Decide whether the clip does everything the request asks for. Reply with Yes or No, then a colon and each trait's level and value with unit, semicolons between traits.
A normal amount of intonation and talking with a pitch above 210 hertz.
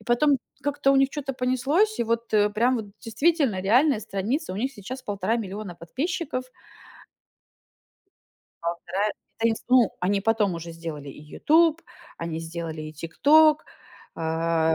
No: wide, 7.9 semitones; high, 220 Hz